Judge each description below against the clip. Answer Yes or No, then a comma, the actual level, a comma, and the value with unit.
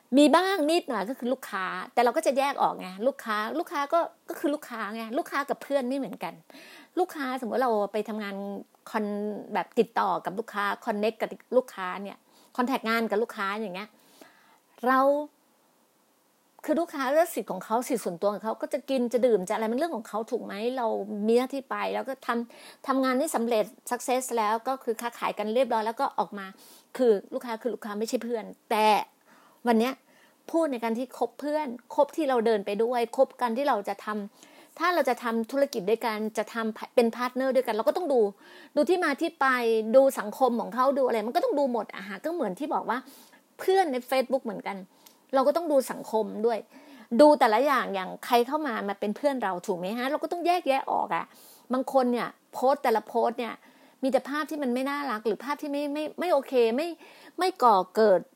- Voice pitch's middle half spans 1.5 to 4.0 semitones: No, average, 4.5 semitones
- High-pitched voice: Yes, very high, 250 Hz